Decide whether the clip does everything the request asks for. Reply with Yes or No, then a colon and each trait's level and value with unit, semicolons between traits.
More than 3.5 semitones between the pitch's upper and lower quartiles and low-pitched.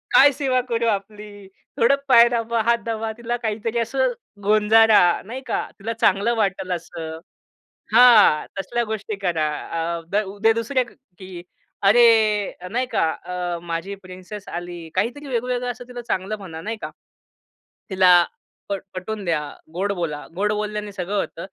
No: average, 4.2 semitones; high, 210 Hz